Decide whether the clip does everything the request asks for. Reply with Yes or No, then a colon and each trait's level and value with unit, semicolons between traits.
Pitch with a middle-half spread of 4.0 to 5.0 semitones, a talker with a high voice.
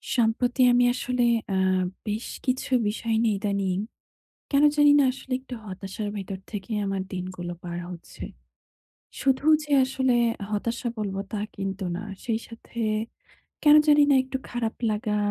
Yes: average, 4.7 semitones; high, 225 Hz